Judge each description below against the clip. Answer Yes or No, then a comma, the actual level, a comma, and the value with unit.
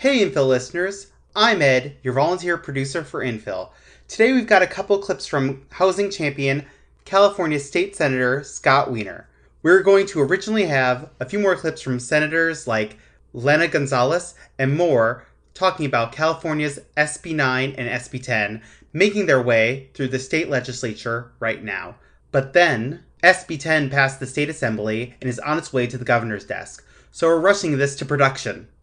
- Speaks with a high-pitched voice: No, medium, 140 Hz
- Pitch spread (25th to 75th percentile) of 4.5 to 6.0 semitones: Yes, average, 5.3 semitones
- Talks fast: No, average, 165 wpm